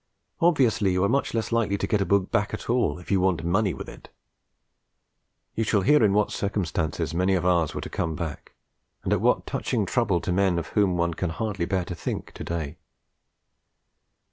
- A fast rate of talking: Yes, fast, 210 wpm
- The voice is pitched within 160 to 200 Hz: No, very low, 95 Hz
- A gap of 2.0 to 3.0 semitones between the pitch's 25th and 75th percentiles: No, average, 3.7 semitones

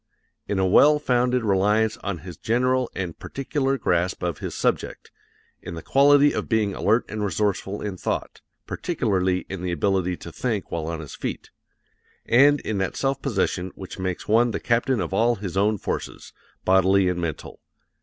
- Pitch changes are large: No, average, 4.8 semitones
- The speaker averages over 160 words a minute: Yes, average, 175 wpm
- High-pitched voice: No, low, 100 Hz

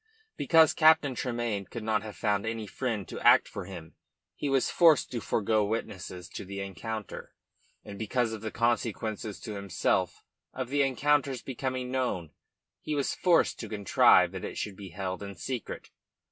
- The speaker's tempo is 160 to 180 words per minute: Yes, average, 170 wpm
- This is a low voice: Yes, low, 110 Hz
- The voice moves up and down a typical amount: Yes, average, 4.5 semitones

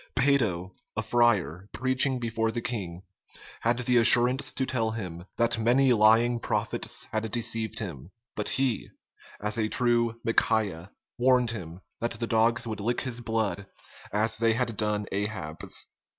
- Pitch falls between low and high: No, low, 115 Hz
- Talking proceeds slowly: No, average, 150 wpm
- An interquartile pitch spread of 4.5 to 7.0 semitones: No, narrow, 2.4 semitones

